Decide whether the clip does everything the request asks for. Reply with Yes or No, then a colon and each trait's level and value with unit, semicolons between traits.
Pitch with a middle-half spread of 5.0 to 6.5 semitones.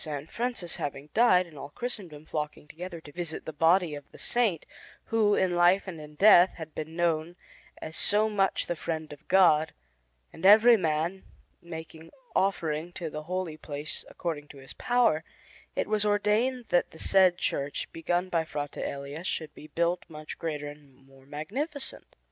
No: average, 4.0 semitones